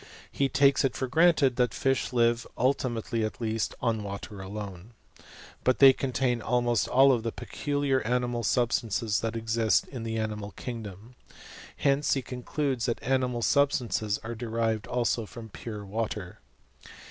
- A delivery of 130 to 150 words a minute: Yes, average, 145 wpm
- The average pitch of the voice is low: Yes, low, 120 Hz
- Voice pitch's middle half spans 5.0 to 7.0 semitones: No, average, 2.9 semitones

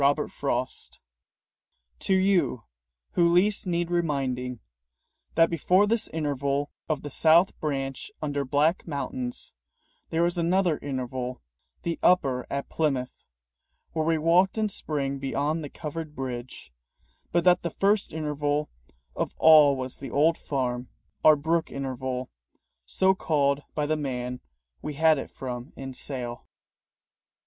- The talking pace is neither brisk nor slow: No, slow, 130 wpm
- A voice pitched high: No, medium, 150 Hz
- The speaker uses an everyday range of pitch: Yes, average, 4.0 semitones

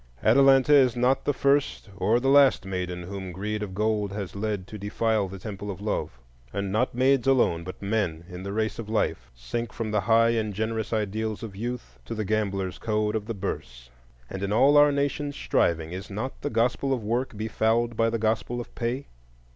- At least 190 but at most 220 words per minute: Yes, average, 200 wpm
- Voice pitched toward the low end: Yes, low, 110 Hz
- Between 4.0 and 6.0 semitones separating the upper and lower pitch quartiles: No, average, 3.4 semitones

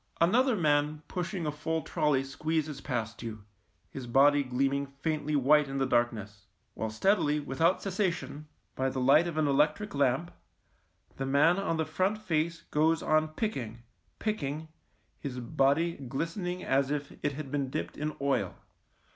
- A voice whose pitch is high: No, medium, 150 Hz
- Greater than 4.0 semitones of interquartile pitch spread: No, average, 3.4 semitones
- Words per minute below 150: No, average, 155 wpm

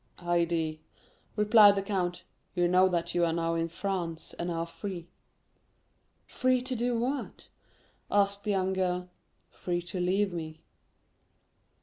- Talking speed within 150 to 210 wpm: No, slow, 135 wpm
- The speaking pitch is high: No, medium, 180 Hz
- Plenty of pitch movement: No, average, 3.0 semitones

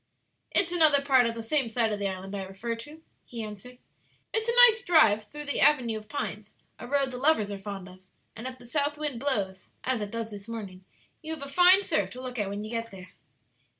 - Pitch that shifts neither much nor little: No, wide, 5.7 semitones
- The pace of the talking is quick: Yes, fast, 235 wpm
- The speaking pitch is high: Yes, high, 235 Hz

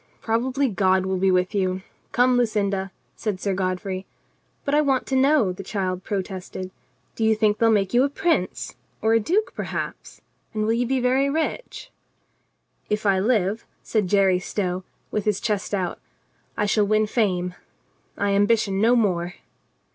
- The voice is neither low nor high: No, high, 210 Hz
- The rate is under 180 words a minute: Yes, average, 170 wpm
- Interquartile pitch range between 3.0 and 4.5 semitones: Yes, average, 3.8 semitones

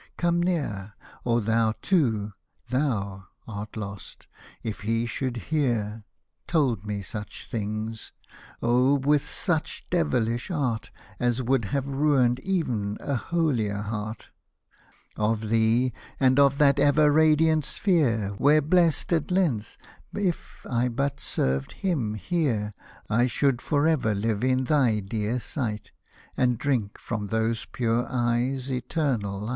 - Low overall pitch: Yes, low, 120 Hz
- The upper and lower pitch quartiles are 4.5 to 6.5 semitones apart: Yes, average, 4.8 semitones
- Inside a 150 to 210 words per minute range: No, slow, 135 wpm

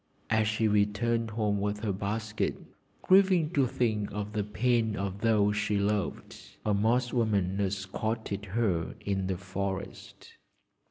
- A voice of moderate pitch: No, low, 105 Hz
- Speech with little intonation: Yes, narrow, 2.1 semitones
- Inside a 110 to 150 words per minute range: Yes, average, 140 wpm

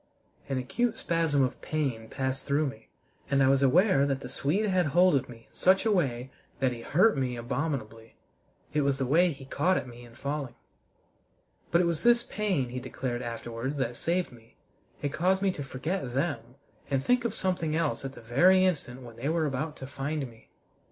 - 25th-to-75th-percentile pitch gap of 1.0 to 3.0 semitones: No, average, 5.1 semitones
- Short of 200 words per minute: No, fast, 205 wpm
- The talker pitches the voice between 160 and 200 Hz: No, medium, 140 Hz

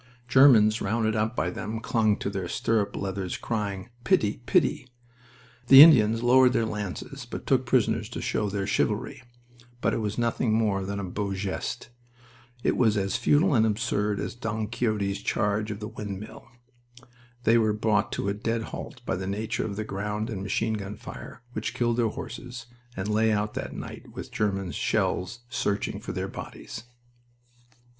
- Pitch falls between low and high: No, low, 110 Hz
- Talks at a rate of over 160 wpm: Yes, average, 170 wpm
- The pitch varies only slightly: Yes, narrow, 2.3 semitones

